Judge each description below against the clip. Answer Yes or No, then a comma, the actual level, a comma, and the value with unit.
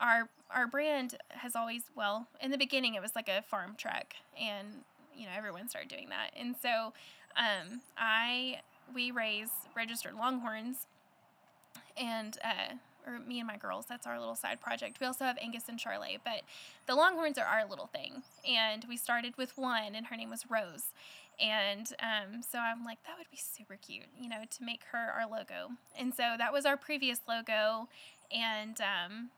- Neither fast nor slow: Yes, average, 185 wpm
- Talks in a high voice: Yes, high, 235 Hz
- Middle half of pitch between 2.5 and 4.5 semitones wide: Yes, average, 3.3 semitones